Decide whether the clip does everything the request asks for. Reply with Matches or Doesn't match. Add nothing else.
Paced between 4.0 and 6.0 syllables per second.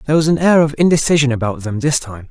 Doesn't match